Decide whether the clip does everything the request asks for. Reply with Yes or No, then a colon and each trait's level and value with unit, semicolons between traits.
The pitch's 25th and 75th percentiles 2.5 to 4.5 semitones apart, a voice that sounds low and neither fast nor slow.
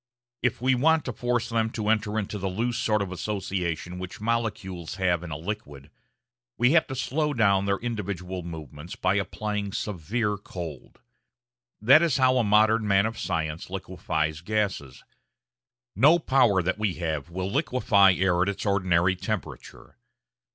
Yes: average, 4.1 semitones; low, 100 Hz; average, 160 wpm